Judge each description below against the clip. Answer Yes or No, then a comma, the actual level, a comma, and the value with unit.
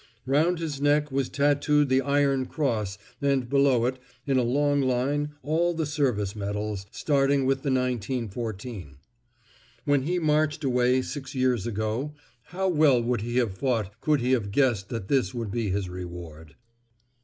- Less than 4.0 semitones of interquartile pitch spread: No, average, 4.3 semitones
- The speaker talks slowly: No, average, 160 wpm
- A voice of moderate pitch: No, low, 130 Hz